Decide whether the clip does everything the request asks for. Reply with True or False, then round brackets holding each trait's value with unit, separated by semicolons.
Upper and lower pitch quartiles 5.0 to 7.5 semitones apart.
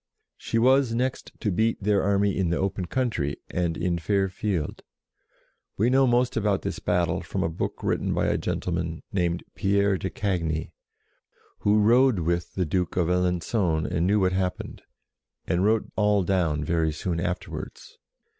False (3.4 semitones)